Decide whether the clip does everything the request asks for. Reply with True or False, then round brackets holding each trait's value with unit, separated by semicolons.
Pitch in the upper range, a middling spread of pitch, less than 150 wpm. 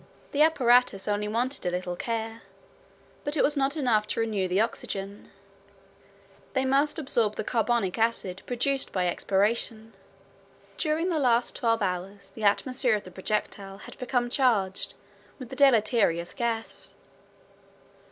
True (225 Hz; 4.4 semitones; 140 wpm)